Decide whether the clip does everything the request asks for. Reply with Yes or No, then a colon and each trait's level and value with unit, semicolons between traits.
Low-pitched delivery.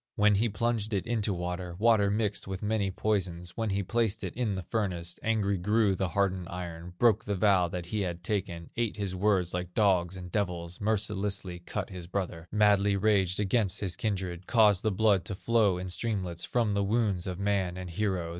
Yes: low, 100 Hz